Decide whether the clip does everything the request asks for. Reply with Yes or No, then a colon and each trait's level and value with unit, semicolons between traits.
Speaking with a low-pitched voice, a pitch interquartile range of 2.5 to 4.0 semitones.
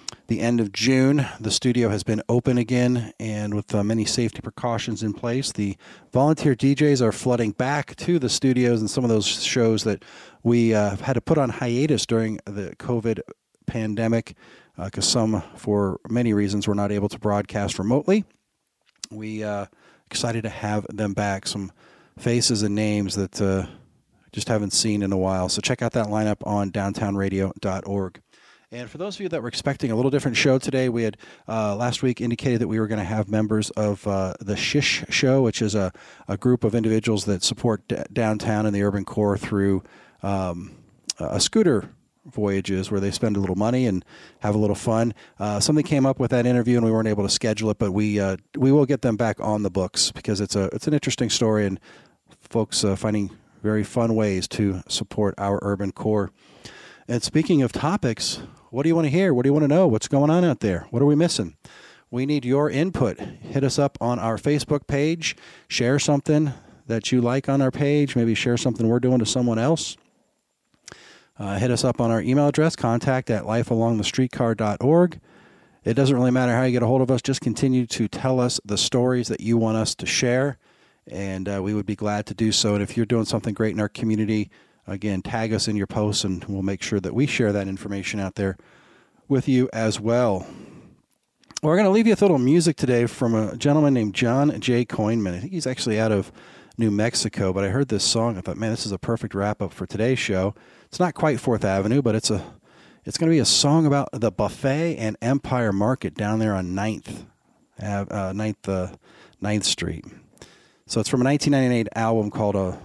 Yes: low, 115 Hz; average, 3.7 semitones